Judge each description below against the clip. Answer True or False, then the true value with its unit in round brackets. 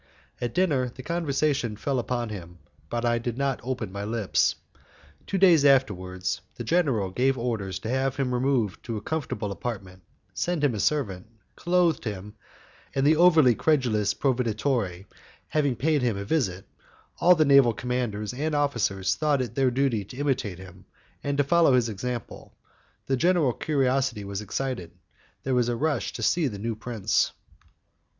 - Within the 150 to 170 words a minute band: True (165 wpm)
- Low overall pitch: True (125 Hz)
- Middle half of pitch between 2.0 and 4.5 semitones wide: False (4.9 semitones)